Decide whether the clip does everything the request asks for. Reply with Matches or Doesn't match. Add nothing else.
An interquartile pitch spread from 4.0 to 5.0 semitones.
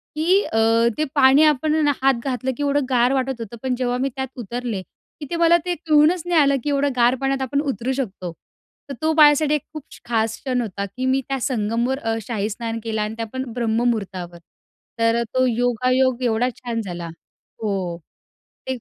Doesn't match